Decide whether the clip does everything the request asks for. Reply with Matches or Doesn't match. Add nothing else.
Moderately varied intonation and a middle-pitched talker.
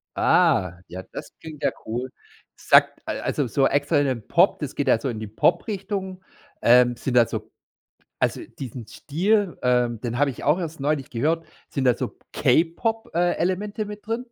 Doesn't match